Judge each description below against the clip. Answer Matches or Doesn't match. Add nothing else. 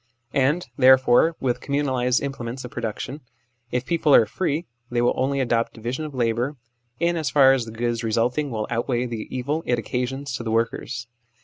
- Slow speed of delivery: Doesn't match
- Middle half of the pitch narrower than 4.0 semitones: Matches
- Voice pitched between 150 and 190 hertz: Doesn't match